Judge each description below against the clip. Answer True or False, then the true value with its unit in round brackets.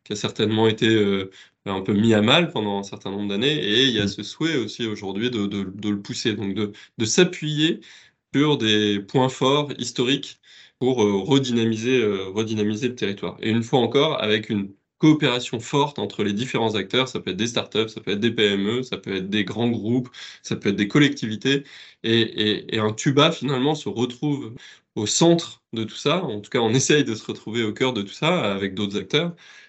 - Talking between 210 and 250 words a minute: True (215 wpm)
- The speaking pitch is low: True (115 Hz)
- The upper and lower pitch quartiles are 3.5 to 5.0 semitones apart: True (4.1 semitones)